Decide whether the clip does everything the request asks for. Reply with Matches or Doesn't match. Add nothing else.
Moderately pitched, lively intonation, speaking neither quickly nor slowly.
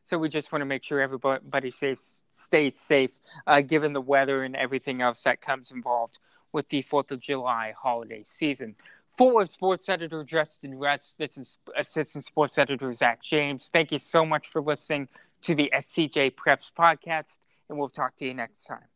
Doesn't match